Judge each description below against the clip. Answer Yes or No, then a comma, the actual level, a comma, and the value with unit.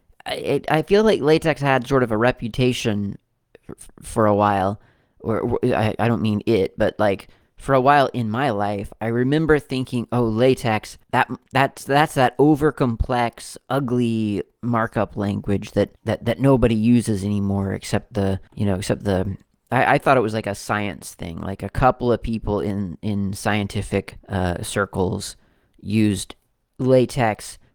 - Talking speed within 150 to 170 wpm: Yes, average, 155 wpm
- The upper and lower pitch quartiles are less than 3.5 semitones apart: No, average, 3.8 semitones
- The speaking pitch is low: Yes, low, 110 Hz